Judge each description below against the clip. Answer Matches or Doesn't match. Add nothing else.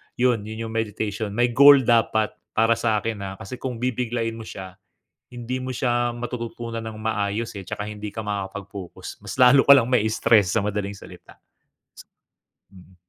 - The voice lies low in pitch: Matches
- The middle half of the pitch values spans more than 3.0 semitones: Doesn't match